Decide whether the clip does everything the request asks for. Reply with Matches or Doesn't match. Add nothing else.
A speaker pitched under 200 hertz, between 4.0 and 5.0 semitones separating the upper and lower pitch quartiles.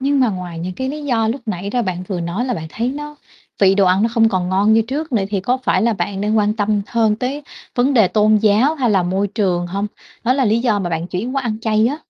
Doesn't match